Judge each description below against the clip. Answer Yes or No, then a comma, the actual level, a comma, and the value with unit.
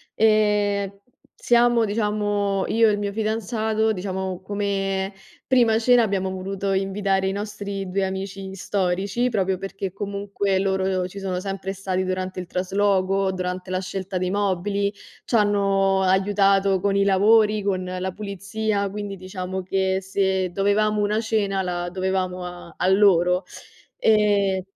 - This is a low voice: No, high, 195 Hz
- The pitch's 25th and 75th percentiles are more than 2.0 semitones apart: No, narrow, 1.5 semitones